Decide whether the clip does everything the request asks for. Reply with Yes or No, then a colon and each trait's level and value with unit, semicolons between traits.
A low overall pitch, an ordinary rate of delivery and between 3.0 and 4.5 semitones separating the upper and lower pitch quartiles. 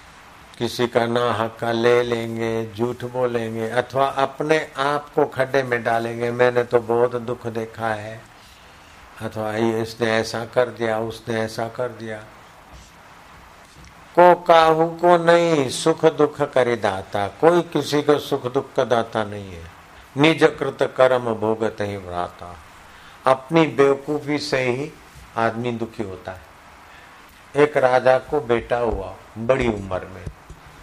Yes: low, 120 Hz; average, 130 wpm; average, 3.7 semitones